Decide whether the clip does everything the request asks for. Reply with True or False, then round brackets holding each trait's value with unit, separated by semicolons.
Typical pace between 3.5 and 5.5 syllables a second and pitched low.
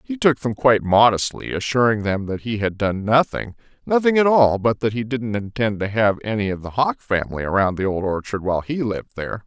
False (5.7 syllables/s; 110 Hz)